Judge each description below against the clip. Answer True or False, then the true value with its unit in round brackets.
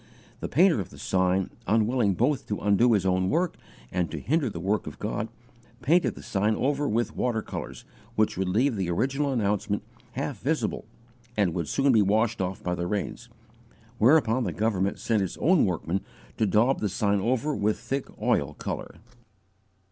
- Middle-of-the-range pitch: False (105 Hz)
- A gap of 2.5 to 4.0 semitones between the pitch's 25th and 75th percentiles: False (4.8 semitones)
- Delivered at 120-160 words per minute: False (180 wpm)